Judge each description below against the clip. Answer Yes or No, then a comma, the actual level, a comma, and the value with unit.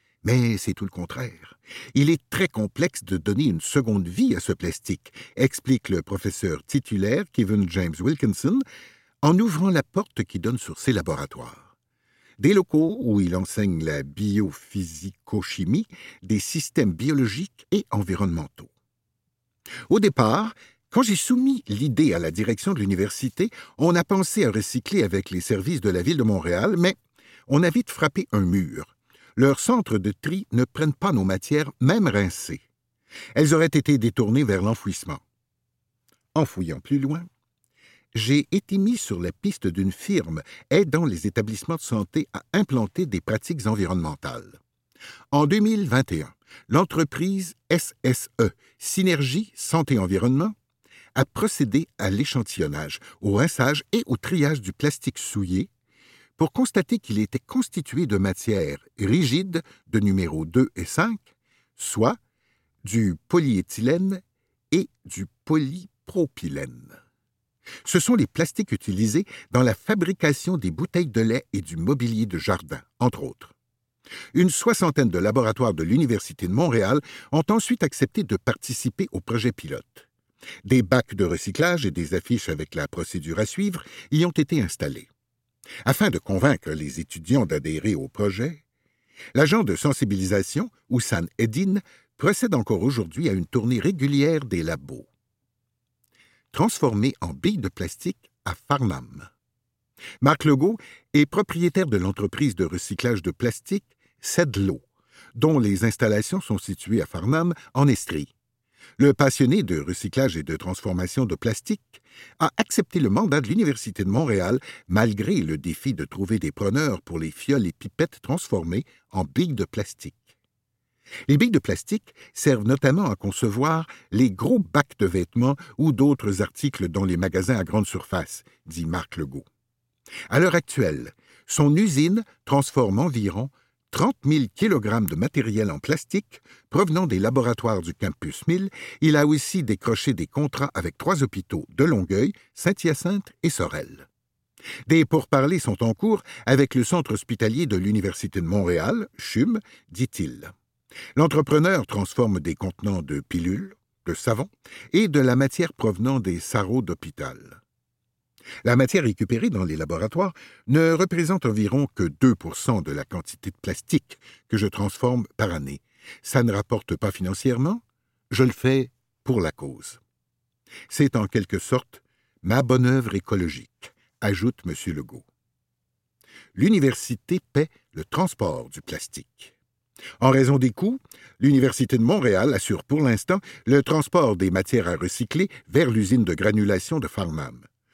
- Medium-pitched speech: No, low, 125 Hz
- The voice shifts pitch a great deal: Yes, wide, 7.5 semitones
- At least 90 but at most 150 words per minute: Yes, slow, 145 wpm